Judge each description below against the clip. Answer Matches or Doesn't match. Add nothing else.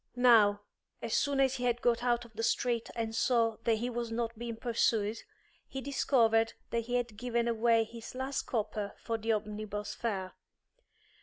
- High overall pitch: Matches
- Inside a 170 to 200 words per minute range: Matches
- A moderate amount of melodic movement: Doesn't match